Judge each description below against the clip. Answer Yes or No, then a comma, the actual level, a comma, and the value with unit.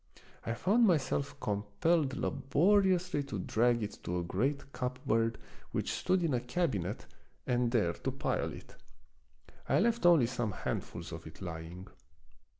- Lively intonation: Yes, wide, 7.8 semitones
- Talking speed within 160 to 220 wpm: No, average, 150 wpm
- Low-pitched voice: Yes, low, 125 Hz